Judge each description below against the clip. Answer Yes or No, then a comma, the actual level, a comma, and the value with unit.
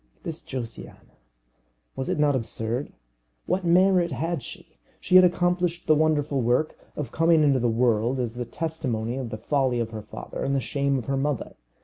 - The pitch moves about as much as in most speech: Yes, average, 4.9 semitones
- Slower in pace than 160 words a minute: No, average, 185 wpm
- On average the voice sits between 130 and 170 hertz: Yes, medium, 140 Hz